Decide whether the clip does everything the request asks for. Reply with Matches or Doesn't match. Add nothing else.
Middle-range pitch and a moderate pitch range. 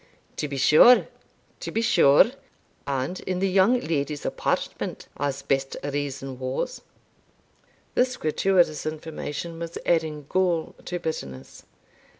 Matches